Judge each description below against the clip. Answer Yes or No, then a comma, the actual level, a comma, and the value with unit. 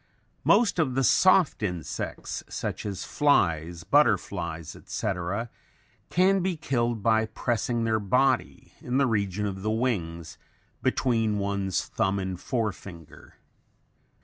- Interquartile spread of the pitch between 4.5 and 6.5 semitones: Yes, average, 5.1 semitones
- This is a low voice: Yes, low, 110 Hz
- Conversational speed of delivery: No, slow, 120 wpm